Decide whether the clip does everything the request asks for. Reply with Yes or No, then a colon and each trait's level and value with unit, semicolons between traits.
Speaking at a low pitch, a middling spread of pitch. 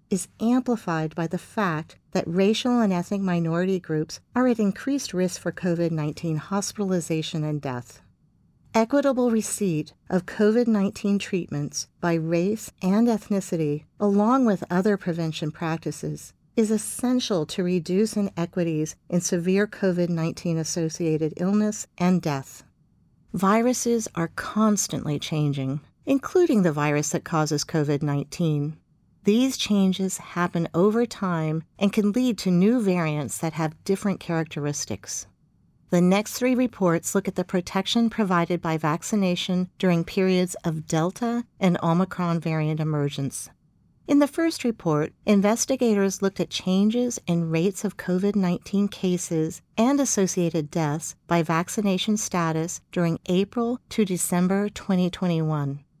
No: medium, 180 Hz; average, 4.2 semitones